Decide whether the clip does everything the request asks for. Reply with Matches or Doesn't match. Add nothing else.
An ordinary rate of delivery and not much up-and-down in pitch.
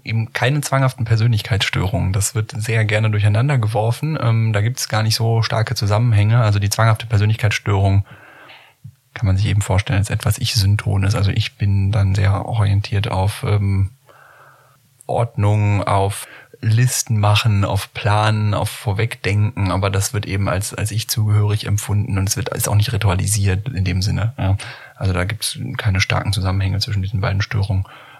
Matches